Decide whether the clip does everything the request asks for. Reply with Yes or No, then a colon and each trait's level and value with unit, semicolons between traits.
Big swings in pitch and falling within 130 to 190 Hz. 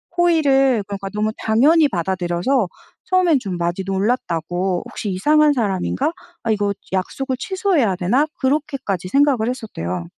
No: wide, 7.1 semitones; high, 220 Hz